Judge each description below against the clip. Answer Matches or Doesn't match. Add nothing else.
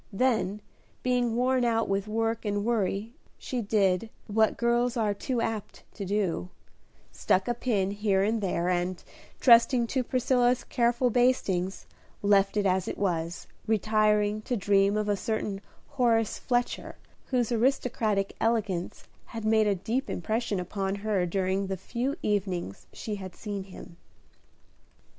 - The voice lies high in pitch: Matches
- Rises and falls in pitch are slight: Doesn't match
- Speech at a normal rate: Matches